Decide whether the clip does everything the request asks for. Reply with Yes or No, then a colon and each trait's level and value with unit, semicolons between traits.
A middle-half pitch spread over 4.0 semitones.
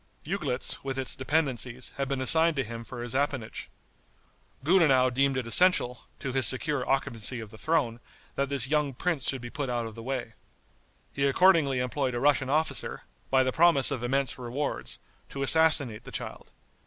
No: average, 2.7 semitones